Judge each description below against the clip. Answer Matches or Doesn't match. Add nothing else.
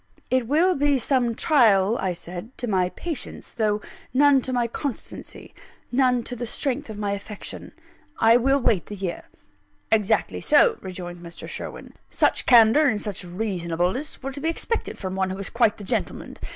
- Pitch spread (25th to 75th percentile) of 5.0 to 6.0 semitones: Matches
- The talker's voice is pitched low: Doesn't match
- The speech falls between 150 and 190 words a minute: Matches